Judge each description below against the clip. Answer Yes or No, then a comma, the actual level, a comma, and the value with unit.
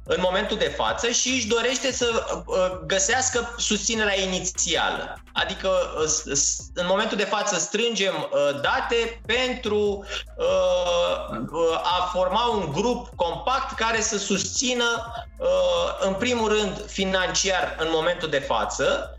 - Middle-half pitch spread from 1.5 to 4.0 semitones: No, average, 4.8 semitones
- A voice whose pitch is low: No, high, 215 Hz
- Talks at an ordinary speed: No, slow, 110 wpm